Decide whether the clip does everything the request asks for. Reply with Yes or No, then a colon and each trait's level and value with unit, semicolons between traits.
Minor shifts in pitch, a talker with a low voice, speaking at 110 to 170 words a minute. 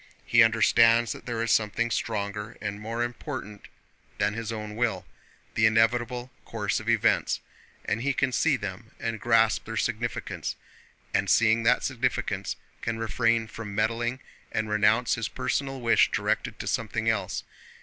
Yes: narrow, 1.7 semitones; low, 115 Hz; average, 150 wpm